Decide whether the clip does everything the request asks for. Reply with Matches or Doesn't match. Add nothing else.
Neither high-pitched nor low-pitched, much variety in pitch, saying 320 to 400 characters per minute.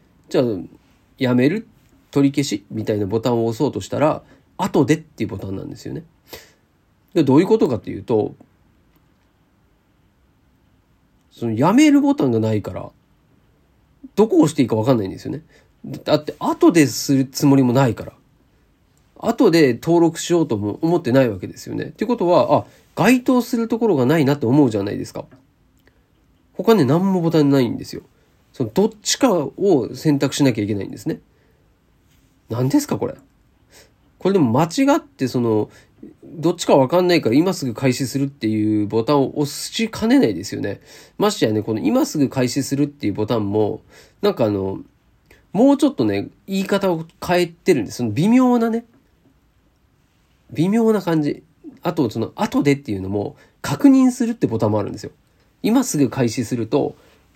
Matches